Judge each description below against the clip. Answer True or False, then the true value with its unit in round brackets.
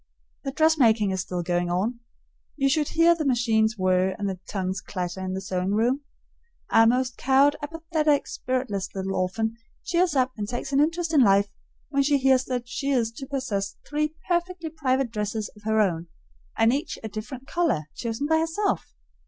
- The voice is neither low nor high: False (245 Hz)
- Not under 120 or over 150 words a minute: False (180 wpm)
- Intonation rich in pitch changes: True (6.3 semitones)